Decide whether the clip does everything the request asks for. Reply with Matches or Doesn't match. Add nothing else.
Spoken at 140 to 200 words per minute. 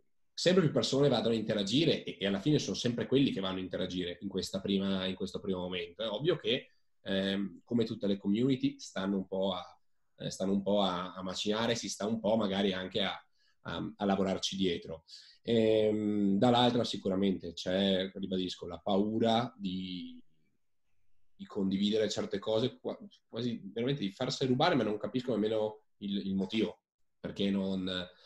Matches